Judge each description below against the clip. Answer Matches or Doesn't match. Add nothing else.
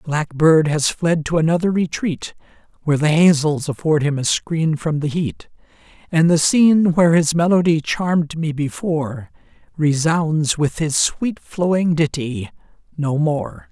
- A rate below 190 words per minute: Matches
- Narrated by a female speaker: Doesn't match